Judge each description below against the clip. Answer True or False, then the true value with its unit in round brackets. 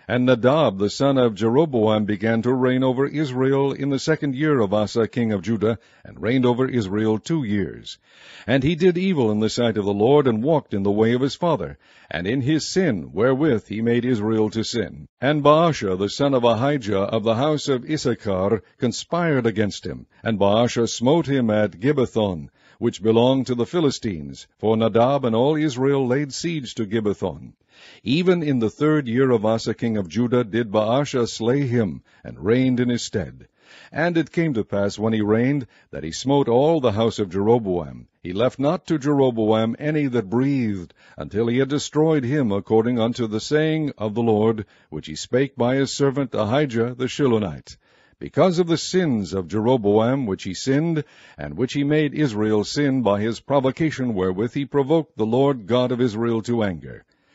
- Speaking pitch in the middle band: False (120 Hz)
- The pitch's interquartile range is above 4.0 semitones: True (4.5 semitones)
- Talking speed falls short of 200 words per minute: True (190 wpm)